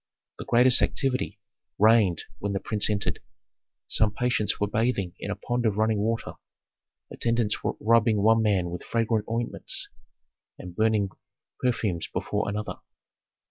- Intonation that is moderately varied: No, narrow, 2.2 semitones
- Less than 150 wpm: Yes, average, 140 wpm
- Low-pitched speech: Yes, low, 110 Hz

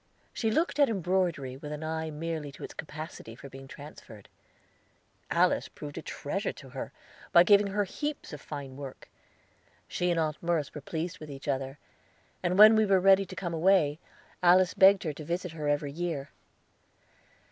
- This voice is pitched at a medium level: Yes, medium, 160 Hz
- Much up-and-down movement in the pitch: No, average, 4.3 semitones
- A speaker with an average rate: Yes, average, 180 wpm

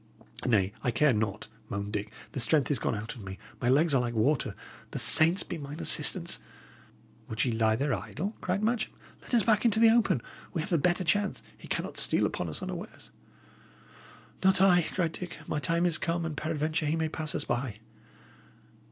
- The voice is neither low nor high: Yes, medium, 155 Hz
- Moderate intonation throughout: No, wide, 6.9 semitones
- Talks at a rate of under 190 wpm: No, average, 195 wpm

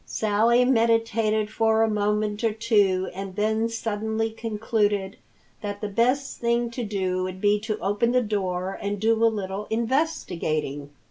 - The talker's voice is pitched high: Yes, high, 215 Hz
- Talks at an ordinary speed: Yes, average, 150 wpm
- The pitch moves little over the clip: Yes, narrow, 2.1 semitones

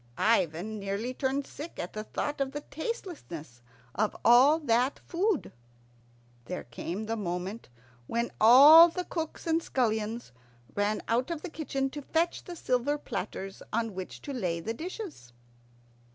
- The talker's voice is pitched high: Yes, high, 245 Hz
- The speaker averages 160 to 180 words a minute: No, average, 150 wpm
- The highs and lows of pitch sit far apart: Yes, wide, 6.3 semitones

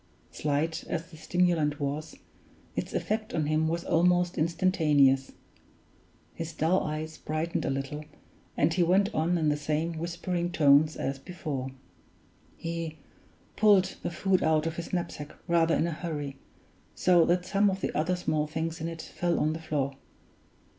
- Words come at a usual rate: Yes, average, 160 wpm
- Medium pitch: Yes, medium, 165 Hz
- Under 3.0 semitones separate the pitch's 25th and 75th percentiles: Yes, narrow, 2.4 semitones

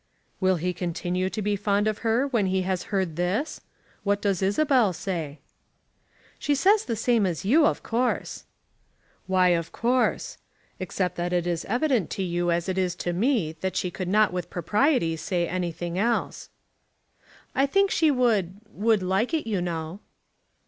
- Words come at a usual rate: Yes, average, 170 wpm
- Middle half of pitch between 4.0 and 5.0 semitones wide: Yes, average, 4.5 semitones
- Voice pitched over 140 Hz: Yes, high, 190 Hz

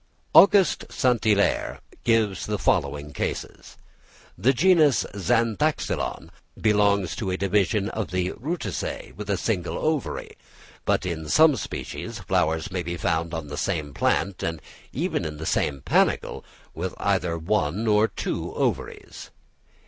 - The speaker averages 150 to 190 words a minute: No, slow, 135 wpm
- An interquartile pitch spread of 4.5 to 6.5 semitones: Yes, average, 5.1 semitones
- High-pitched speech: No, low, 100 Hz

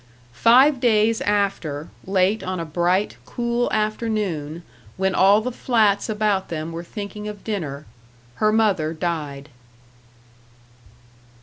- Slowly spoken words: Yes, slow, 115 wpm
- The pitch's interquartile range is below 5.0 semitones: Yes, average, 4.4 semitones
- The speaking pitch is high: Yes, high, 200 Hz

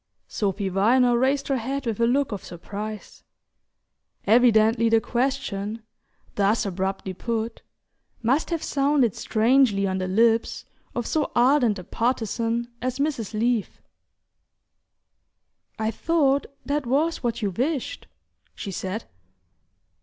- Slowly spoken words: Yes, slow, 120 wpm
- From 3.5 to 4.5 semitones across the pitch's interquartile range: Yes, average, 4.0 semitones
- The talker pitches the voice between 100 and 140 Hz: No, high, 230 Hz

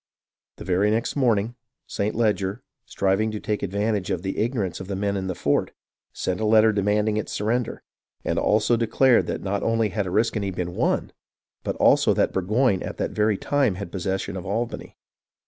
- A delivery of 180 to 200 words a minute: Yes, average, 185 wpm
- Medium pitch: No, low, 105 Hz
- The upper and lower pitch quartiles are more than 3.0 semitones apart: No, narrow, 2.6 semitones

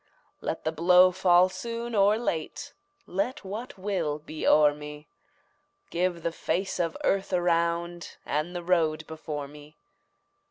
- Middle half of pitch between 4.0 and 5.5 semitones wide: No, average, 3.3 semitones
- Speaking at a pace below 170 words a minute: Yes, slow, 135 wpm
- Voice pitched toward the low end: No, medium, 175 Hz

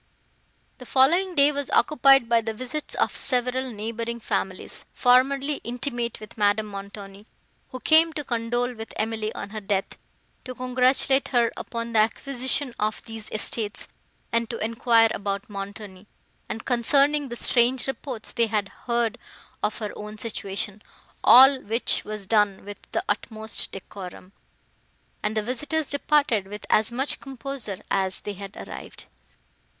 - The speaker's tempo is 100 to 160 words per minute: Yes, average, 145 wpm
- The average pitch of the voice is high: Yes, high, 230 Hz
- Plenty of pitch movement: No, average, 3.6 semitones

